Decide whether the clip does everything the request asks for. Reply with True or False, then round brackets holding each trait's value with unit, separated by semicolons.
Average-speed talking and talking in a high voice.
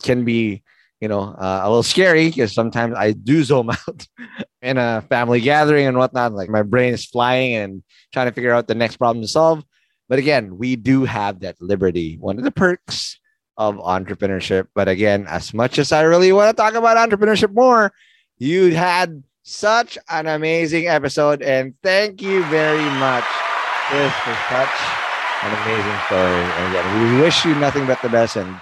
False (180 wpm; 125 Hz)